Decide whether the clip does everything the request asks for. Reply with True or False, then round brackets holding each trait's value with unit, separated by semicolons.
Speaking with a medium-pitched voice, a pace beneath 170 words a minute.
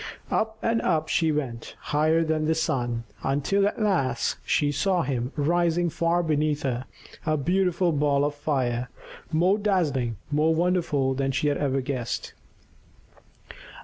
True (150 Hz; 145 wpm)